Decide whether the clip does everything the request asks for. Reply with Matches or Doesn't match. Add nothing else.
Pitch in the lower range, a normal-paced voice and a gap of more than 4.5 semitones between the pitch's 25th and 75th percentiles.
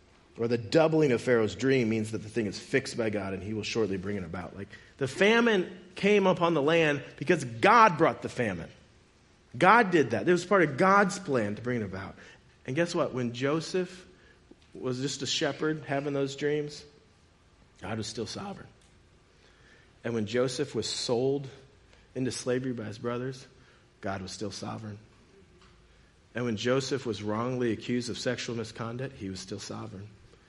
Matches